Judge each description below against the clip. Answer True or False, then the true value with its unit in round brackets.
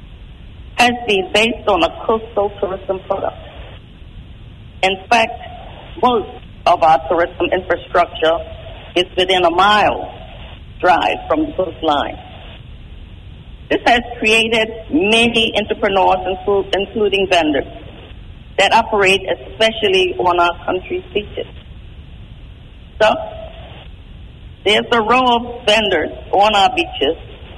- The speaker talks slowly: True (100 wpm)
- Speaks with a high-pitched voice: True (195 Hz)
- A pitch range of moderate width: False (6.2 semitones)